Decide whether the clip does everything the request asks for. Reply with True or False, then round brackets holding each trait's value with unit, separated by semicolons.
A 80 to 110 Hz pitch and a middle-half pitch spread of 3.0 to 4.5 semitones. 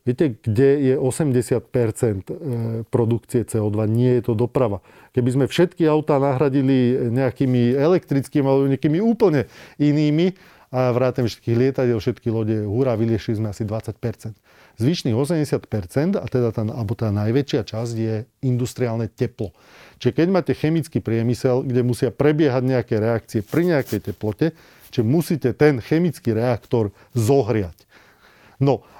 False (125 Hz; 3.6 semitones)